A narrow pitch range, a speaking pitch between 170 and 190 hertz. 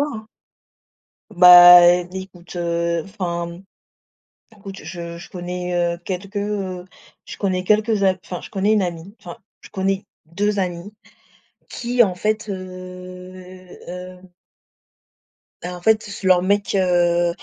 Yes: narrow, 2.1 semitones; medium, 185 Hz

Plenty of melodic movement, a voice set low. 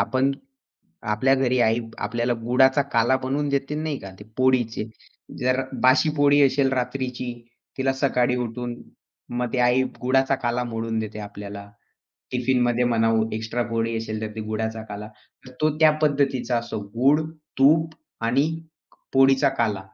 No: average, 2.9 semitones; low, 125 Hz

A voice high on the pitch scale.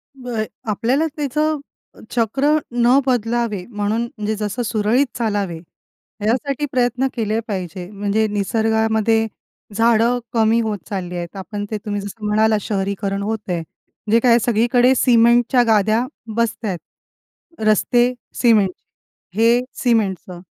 Yes: high, 220 Hz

